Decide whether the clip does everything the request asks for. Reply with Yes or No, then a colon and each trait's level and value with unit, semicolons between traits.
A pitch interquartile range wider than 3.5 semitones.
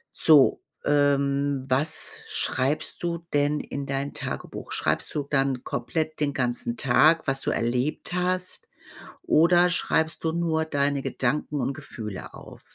No: average, 2.8 semitones